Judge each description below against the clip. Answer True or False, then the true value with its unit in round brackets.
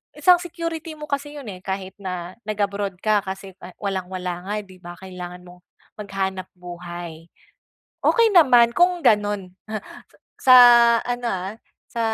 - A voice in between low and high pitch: False (195 Hz)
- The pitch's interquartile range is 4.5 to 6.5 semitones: True (5.2 semitones)